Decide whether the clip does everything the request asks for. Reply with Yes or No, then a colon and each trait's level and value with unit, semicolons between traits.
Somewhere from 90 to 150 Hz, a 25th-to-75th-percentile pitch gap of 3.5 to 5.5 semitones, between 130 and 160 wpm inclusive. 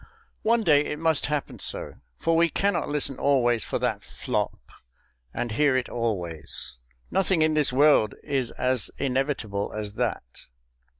Yes: low, 135 Hz; average, 4.9 semitones; average, 145 wpm